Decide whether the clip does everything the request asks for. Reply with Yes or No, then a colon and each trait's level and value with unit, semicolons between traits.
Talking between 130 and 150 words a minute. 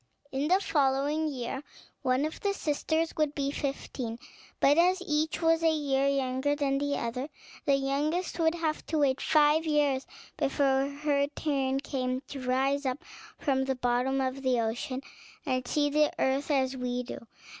No: average, 165 wpm